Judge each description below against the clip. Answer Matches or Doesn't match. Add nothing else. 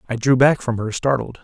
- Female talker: Doesn't match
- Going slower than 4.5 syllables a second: Doesn't match